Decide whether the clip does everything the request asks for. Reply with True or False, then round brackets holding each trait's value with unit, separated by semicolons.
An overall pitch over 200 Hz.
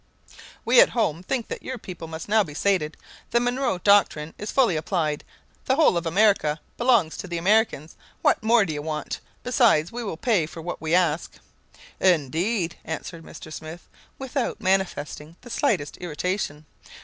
False (180 Hz)